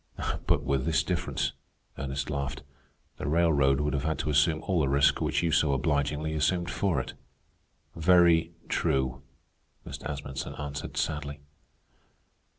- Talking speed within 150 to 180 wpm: No, average, 140 wpm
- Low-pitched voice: Yes, very low, 75 Hz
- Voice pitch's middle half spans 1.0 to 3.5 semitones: Yes, average, 2.8 semitones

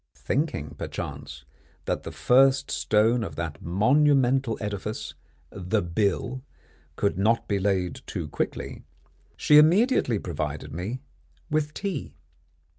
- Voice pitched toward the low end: Yes, low, 110 Hz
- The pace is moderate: No, slow, 115 wpm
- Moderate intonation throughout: No, wide, 7.2 semitones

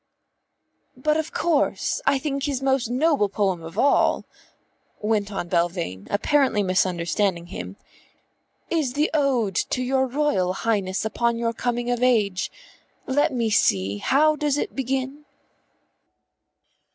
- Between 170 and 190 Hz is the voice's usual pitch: No, high, 235 Hz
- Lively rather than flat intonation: Yes, wide, 6.3 semitones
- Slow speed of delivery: Yes, slow, 125 wpm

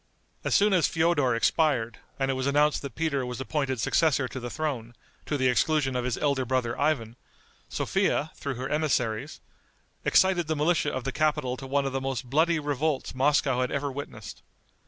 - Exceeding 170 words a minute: Yes, average, 185 wpm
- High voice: No, low, 135 Hz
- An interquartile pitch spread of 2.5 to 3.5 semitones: Yes, average, 3.1 semitones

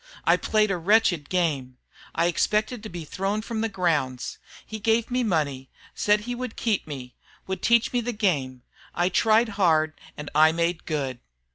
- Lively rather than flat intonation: Yes, wide, 6.1 semitones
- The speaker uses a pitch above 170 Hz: Yes, medium, 185 Hz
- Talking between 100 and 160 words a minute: No, average, 175 wpm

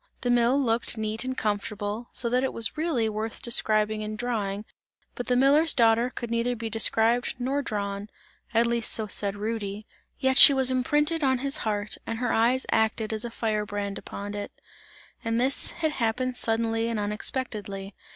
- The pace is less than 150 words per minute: No, average, 180 wpm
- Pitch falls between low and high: No, high, 230 Hz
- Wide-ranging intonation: No, average, 2.9 semitones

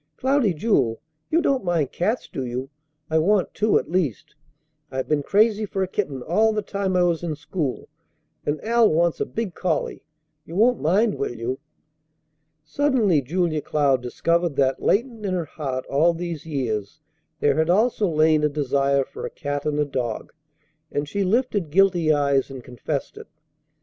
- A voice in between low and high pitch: Yes, medium, 160 Hz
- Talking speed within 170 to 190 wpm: Yes, average, 175 wpm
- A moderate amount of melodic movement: No, wide, 5.9 semitones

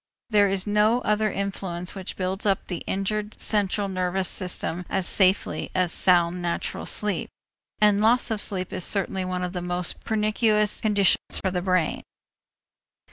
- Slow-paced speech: No, average, 155 wpm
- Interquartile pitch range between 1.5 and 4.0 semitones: Yes, narrow, 2.4 semitones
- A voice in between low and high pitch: No, high, 195 Hz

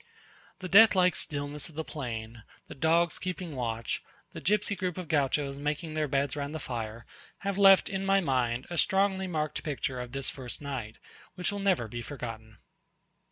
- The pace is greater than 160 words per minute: Yes, average, 180 wpm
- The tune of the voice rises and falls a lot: Yes, wide, 6.4 semitones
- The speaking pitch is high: No, medium, 150 Hz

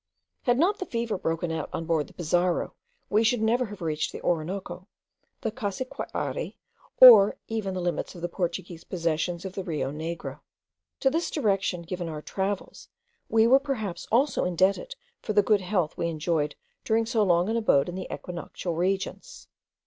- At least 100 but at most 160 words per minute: No, average, 175 wpm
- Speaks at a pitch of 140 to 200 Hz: Yes, high, 190 Hz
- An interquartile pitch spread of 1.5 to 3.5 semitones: No, average, 4.7 semitones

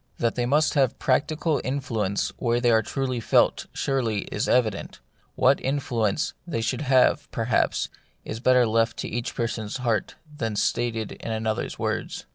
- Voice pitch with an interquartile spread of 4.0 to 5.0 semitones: No, average, 2.9 semitones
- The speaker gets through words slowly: No, average, 155 wpm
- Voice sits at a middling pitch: No, low, 120 Hz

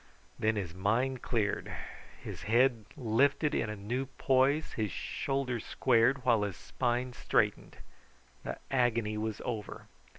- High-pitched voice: No, low, 120 Hz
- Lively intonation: No, average, 3.4 semitones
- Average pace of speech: No, slow, 130 wpm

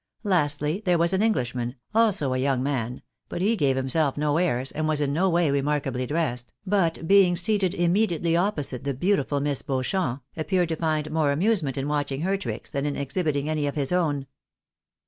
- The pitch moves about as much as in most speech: Yes, average, 4.3 semitones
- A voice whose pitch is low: No, medium, 150 Hz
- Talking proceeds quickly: No, average, 185 wpm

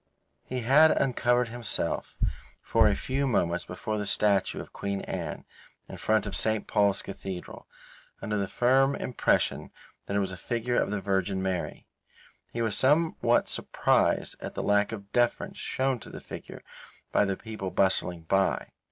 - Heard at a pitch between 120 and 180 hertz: No, low, 105 Hz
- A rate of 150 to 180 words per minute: Yes, average, 160 wpm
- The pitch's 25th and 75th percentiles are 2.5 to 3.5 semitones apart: No, average, 3.9 semitones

